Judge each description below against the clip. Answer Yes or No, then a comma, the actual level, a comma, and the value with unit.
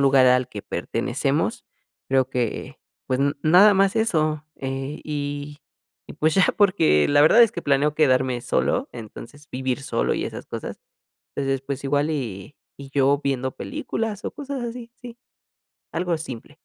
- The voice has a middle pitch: Yes, medium, 145 Hz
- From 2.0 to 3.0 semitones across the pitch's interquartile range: No, average, 4.8 semitones